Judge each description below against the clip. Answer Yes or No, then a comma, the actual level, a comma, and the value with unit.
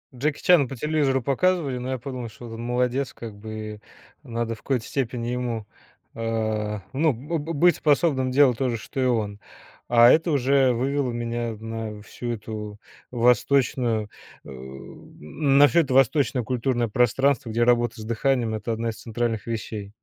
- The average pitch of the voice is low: Yes, low, 120 Hz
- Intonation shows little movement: No, average, 3.2 semitones